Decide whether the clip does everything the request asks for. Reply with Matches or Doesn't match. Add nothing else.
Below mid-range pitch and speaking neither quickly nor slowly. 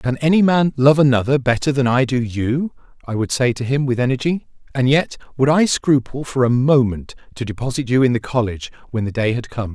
Doesn't match